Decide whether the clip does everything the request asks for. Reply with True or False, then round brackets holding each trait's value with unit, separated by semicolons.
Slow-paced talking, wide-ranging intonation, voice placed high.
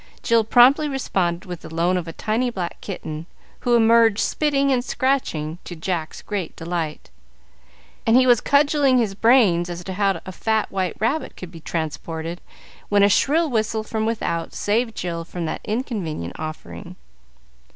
False (160 wpm; 5.9 semitones; 205 Hz)